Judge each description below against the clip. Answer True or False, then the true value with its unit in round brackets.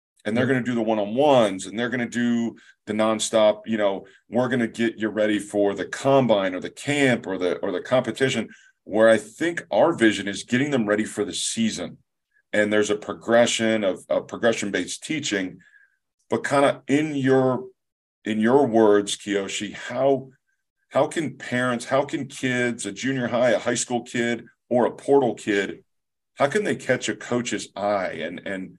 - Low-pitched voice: True (115 Hz)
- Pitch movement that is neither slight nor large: True (3.5 semitones)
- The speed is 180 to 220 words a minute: True (185 wpm)